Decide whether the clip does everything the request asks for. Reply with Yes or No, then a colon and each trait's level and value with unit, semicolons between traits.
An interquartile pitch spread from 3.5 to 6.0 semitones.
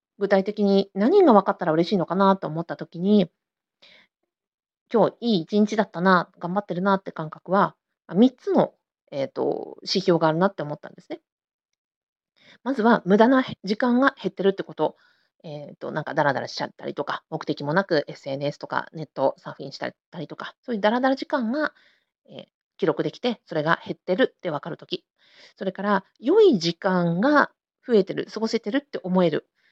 Yes: average, 5.3 semitones